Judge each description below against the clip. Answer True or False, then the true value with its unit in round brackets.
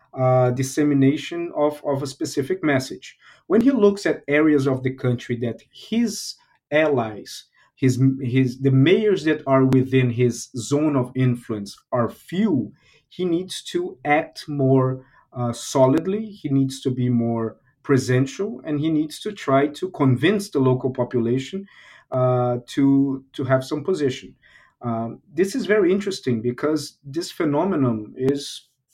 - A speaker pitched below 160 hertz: True (135 Hz)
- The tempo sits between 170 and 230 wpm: False (145 wpm)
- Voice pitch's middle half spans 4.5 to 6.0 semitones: False (3.3 semitones)